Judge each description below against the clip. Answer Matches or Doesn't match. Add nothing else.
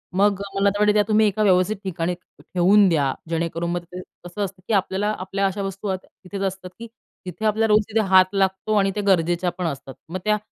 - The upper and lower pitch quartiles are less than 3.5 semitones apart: Matches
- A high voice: Matches